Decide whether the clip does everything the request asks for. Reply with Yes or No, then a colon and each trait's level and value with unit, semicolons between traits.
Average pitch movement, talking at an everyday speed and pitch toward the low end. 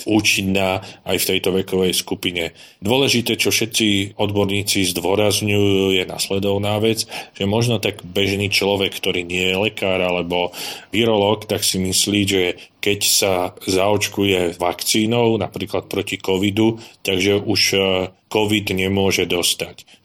No: narrow, 2.0 semitones; average, 125 wpm; low, 100 Hz